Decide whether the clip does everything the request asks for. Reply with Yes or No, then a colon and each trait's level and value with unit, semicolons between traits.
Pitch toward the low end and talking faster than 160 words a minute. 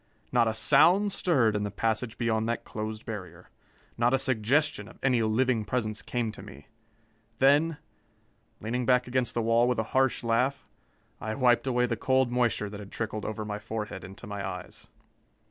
Yes: low, 115 Hz; average, 180 wpm